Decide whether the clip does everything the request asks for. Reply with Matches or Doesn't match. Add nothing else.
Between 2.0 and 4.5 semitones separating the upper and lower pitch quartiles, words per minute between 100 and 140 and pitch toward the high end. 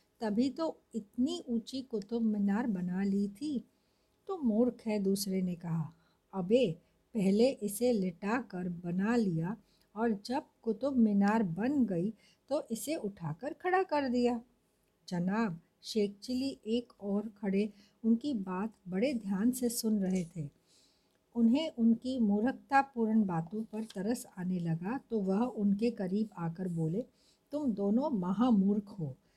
Matches